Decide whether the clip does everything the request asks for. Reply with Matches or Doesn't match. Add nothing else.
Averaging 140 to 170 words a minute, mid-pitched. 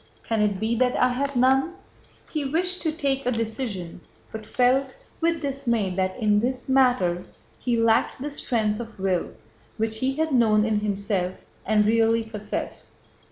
Doesn't match